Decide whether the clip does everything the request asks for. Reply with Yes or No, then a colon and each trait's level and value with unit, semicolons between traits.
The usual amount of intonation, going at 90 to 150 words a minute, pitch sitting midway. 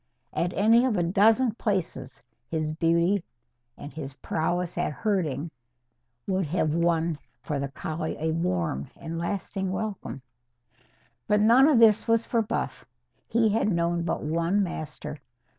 Yes: average, 4.8 semitones; average, 140 wpm; medium, 170 Hz